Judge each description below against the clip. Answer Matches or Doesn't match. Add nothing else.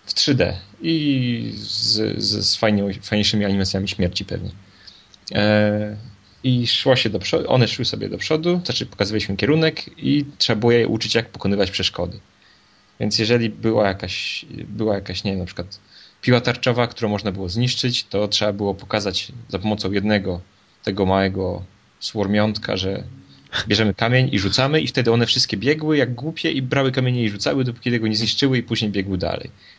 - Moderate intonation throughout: Matches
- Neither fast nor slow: Doesn't match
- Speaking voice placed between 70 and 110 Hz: Matches